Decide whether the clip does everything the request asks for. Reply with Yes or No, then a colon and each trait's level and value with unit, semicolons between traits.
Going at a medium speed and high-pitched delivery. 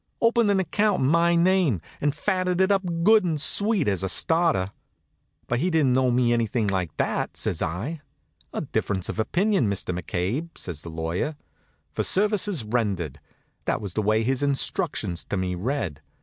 No: average, 175 wpm; low, 130 Hz